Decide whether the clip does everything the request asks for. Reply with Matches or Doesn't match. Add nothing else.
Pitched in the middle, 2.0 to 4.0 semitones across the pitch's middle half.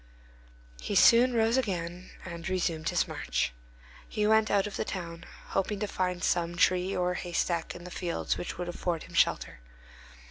Matches